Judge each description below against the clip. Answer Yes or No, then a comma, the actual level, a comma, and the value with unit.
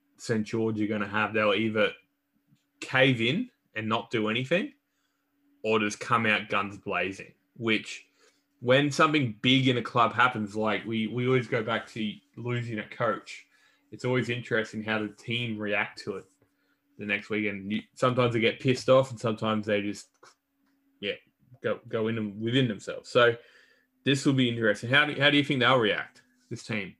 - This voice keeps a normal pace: Yes, average, 180 wpm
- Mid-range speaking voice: No, low, 115 Hz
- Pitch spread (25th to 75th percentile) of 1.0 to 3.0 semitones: No, average, 3.5 semitones